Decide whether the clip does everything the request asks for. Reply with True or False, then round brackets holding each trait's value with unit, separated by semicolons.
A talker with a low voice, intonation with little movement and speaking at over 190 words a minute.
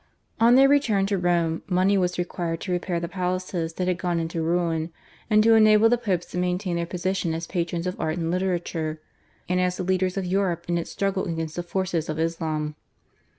False (180 Hz; 2.1 semitones; 205 wpm)